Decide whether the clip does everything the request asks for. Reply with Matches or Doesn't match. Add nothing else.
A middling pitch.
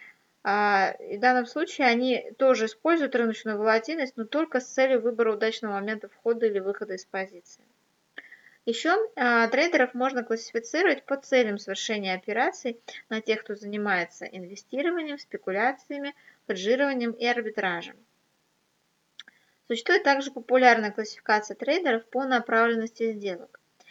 Doesn't match